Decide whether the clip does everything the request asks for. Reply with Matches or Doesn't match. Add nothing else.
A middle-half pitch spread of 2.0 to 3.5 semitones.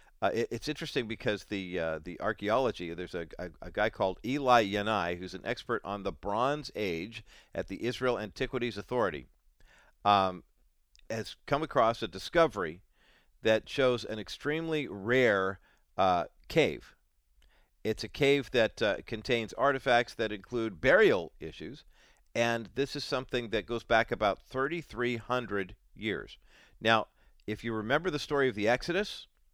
Doesn't match